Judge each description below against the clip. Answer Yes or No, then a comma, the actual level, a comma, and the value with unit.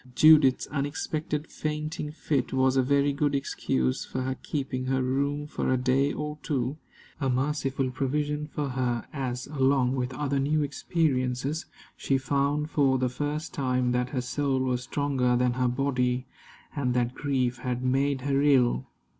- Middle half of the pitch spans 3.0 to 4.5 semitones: No, narrow, 2.4 semitones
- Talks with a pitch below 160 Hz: Yes, low, 135 Hz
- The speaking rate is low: No, average, 160 wpm